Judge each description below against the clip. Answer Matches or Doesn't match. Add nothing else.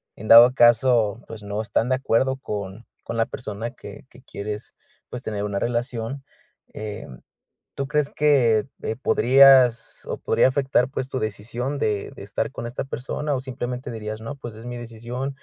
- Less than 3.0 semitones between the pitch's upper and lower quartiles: Doesn't match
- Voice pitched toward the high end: Doesn't match